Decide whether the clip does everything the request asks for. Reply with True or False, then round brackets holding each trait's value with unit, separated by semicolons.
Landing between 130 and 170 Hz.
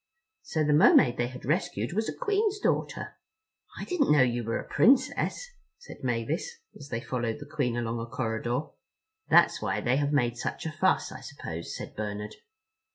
True (135 Hz)